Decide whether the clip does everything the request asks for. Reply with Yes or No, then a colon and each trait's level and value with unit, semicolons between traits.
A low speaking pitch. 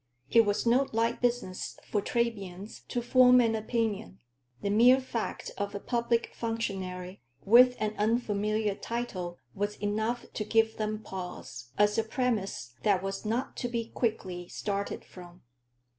No: high, 215 Hz